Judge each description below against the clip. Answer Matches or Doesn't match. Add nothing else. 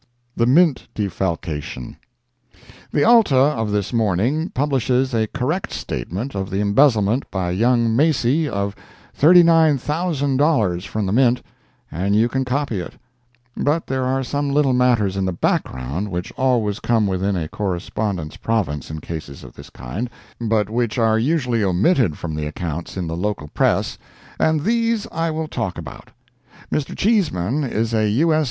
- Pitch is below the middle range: Matches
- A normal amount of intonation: Doesn't match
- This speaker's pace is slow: Doesn't match